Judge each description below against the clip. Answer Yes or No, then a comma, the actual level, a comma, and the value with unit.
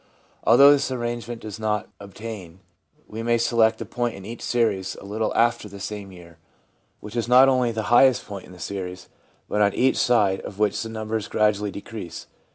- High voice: No, low, 110 Hz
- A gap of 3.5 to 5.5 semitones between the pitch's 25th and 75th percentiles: No, average, 2.8 semitones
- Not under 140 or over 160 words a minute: No, average, 195 wpm